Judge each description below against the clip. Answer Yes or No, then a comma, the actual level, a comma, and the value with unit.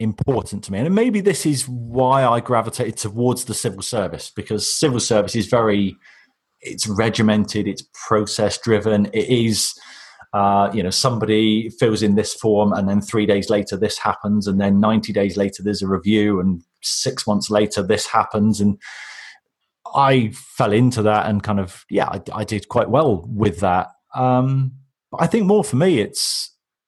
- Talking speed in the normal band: Yes, average, 175 wpm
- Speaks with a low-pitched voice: Yes, low, 105 Hz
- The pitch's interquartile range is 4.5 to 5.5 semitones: No, narrow, 2.6 semitones